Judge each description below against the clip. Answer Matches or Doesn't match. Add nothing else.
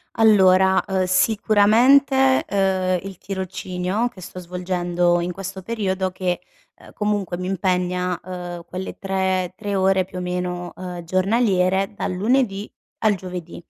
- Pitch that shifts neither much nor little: Doesn't match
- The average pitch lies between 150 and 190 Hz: Matches